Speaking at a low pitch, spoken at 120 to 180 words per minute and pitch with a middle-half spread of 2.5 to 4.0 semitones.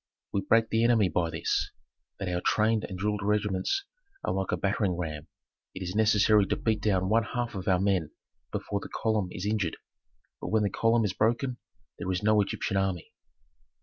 No: low, 100 Hz; average, 190 wpm; average, 2.9 semitones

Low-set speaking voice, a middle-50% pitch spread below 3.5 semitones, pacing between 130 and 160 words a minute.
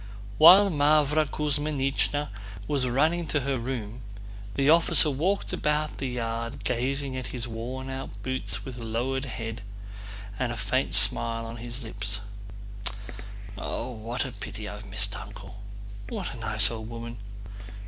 No: low, 125 Hz; average, 3.8 semitones; average, 140 wpm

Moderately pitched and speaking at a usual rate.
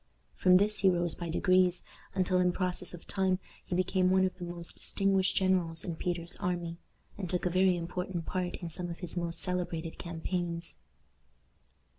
Yes: medium, 180 Hz; average, 175 wpm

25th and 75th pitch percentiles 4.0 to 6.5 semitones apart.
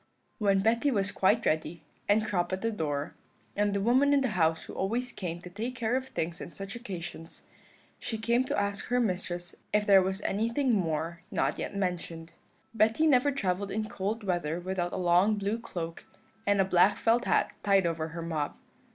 Yes: average, 4.3 semitones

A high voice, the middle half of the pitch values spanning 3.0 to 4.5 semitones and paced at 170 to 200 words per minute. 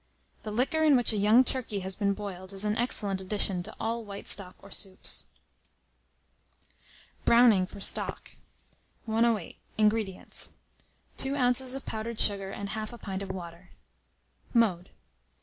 No: high, 210 Hz; average, 3.3 semitones; average, 145 wpm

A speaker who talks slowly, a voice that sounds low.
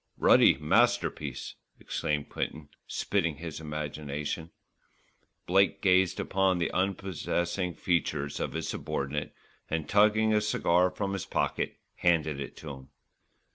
Yes: slow, 120 wpm; very low, 85 Hz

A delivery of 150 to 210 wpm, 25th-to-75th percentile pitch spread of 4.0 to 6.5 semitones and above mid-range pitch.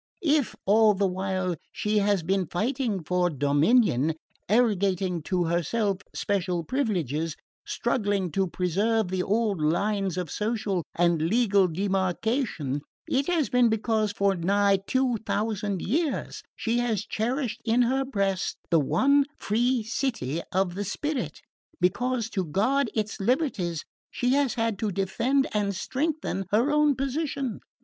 No: slow, 135 wpm; average, 4.9 semitones; high, 205 Hz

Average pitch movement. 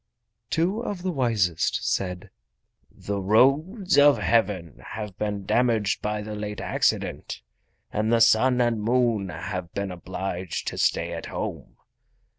Yes: average, 4.4 semitones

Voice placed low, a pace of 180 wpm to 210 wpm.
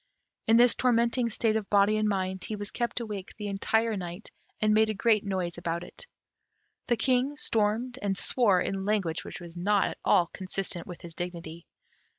No: high, 205 Hz; average, 185 wpm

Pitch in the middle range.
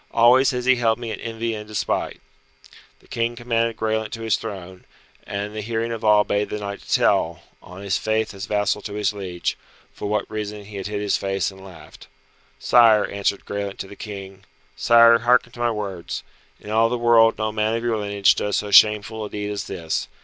No: low, 105 Hz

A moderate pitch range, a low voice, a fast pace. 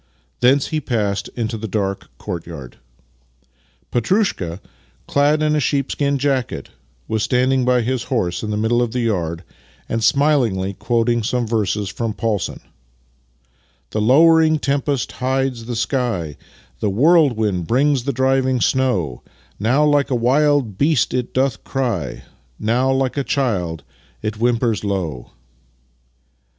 No: average, 4.5 semitones; low, 120 Hz; slow, 135 wpm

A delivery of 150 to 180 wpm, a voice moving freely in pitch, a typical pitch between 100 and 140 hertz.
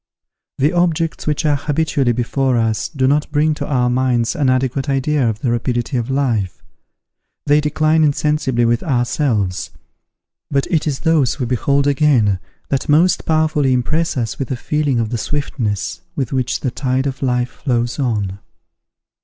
No: average, 160 wpm; average, 3.7 semitones; low, 135 Hz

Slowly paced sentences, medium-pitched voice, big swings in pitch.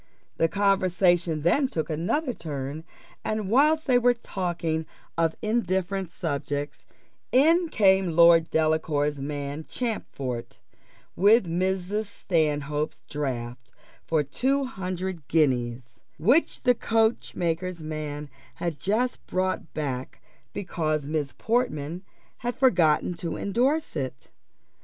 Yes: slow, 105 wpm; medium, 170 Hz; wide, 6.0 semitones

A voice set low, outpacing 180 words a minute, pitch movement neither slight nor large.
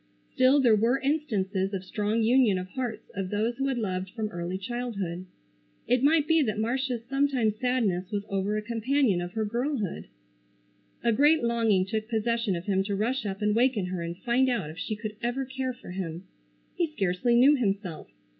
No: high, 220 Hz; average, 190 wpm; average, 4.6 semitones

